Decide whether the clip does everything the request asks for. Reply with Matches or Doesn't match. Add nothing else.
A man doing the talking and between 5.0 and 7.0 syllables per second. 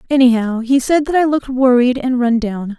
Doesn't match